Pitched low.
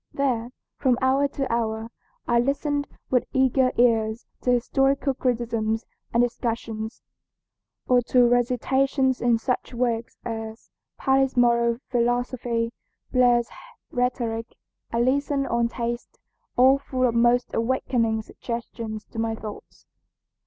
No: high, 240 Hz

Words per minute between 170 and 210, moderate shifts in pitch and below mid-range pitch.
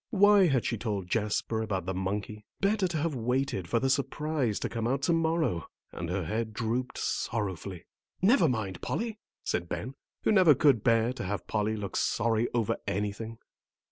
No: average, 175 wpm; wide, 6.0 semitones; low, 115 Hz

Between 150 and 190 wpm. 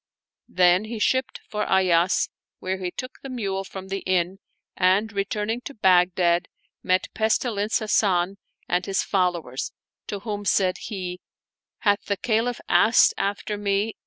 Yes: average, 155 wpm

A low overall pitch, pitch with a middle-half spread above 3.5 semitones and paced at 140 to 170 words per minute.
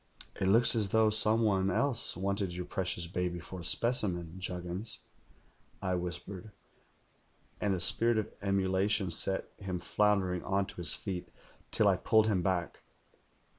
No: very low, 95 Hz; average, 2.8 semitones; average, 150 wpm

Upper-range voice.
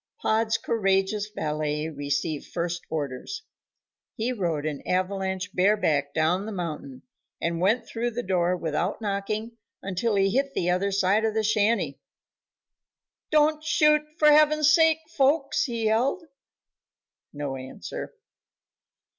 Yes: high, 200 Hz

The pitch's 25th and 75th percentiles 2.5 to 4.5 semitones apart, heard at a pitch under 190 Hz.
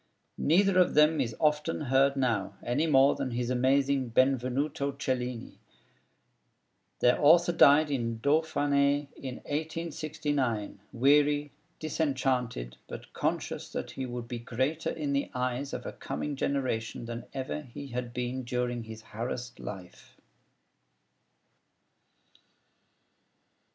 Yes: average, 3.1 semitones; low, 135 Hz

